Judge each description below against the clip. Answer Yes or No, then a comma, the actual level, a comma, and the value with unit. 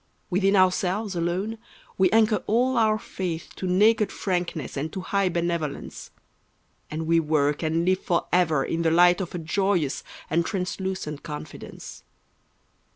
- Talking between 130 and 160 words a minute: Yes, average, 140 wpm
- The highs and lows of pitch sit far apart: No, average, 3.1 semitones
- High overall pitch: No, medium, 180 Hz